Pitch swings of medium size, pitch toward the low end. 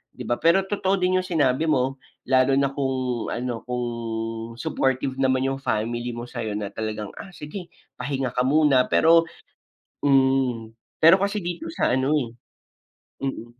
Yes: average, 4.1 semitones; low, 130 Hz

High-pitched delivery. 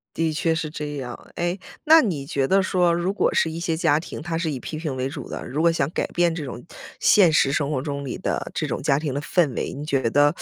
No: medium, 155 Hz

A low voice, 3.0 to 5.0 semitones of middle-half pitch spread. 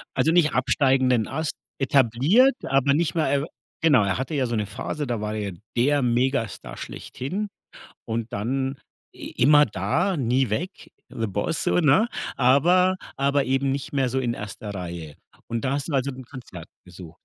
Yes: low, 130 Hz; average, 4.0 semitones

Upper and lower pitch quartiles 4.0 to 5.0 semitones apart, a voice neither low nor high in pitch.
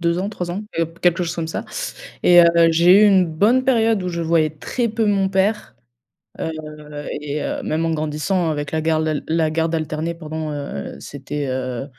No: average, 3.4 semitones; medium, 165 Hz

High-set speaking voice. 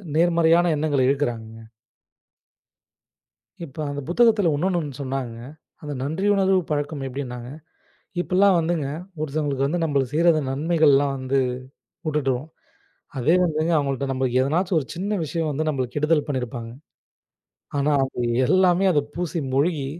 No: medium, 150 Hz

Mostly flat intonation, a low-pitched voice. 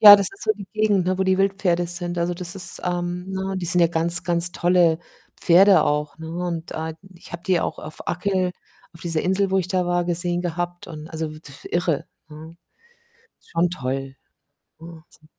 No: narrow, 2.0 semitones; medium, 175 Hz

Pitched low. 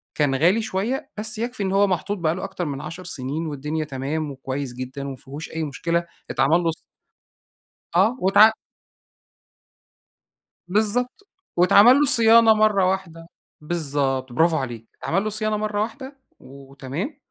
No: medium, 170 Hz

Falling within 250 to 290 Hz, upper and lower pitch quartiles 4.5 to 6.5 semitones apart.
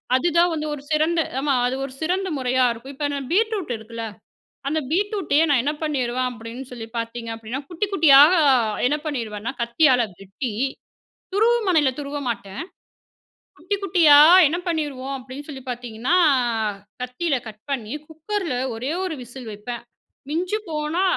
Yes: very high, 280 Hz; average, 5.1 semitones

